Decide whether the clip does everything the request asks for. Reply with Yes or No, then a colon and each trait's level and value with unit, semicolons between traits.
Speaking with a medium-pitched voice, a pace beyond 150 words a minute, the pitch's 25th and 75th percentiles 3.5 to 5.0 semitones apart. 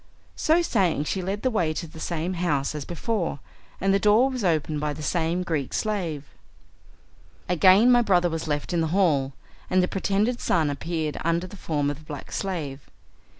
Yes: medium, 170 Hz; average, 190 wpm; average, 4.2 semitones